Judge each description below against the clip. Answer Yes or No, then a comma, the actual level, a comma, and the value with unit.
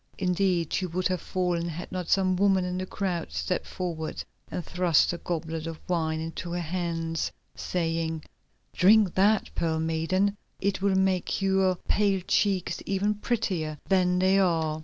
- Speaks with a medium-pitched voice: Yes, medium, 180 Hz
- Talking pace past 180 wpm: No, average, 160 wpm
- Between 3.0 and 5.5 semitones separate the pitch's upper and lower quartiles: No, narrow, 2.6 semitones